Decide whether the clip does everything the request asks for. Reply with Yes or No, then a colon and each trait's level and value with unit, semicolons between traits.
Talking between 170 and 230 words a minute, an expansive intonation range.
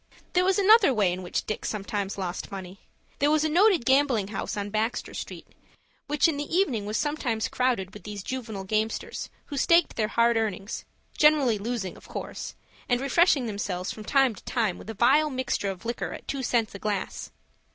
Yes: average, 195 wpm; wide, 5.9 semitones